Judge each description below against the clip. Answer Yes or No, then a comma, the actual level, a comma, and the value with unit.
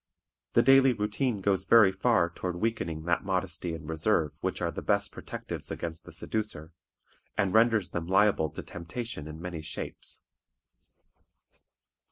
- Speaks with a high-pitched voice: No, very low, 95 Hz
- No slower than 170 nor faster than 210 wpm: No, average, 145 wpm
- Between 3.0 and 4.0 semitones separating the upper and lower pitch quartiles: No, average, 4.7 semitones